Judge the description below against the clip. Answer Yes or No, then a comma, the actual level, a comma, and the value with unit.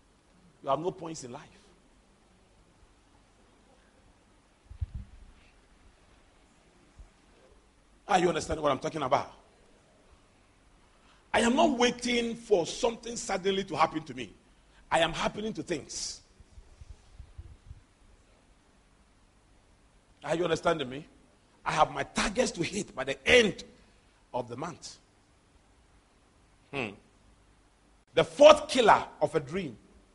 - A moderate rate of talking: No, slow, 105 wpm